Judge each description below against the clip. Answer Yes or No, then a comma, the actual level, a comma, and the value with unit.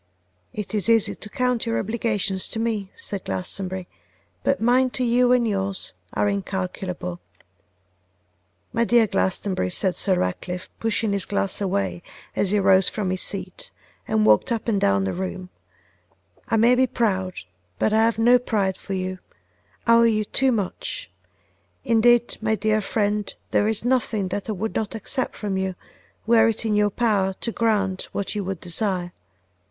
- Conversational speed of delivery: Yes, average, 170 wpm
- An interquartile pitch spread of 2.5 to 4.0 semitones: Yes, average, 3.3 semitones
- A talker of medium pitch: No, high, 205 Hz